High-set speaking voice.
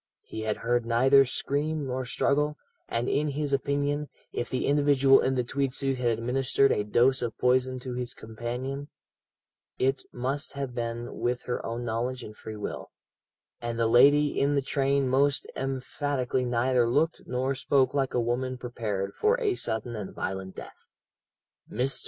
No: low, 130 Hz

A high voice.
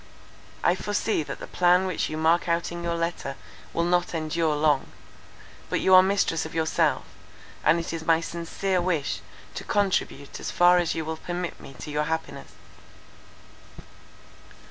No: medium, 170 Hz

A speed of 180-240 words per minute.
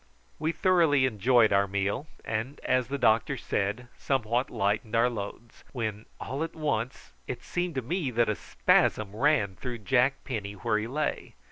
No: average, 165 wpm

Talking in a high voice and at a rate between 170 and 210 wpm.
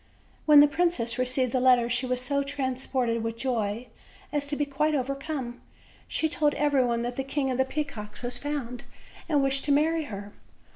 Yes: very high, 265 Hz; average, 195 wpm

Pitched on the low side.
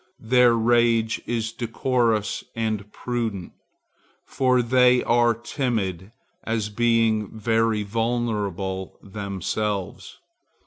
Yes: low, 115 Hz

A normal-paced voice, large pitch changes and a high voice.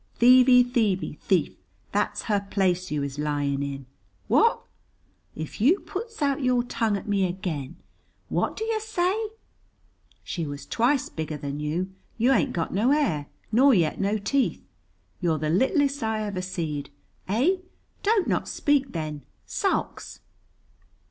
Yes: average, 145 wpm; wide, 9.0 semitones; high, 205 Hz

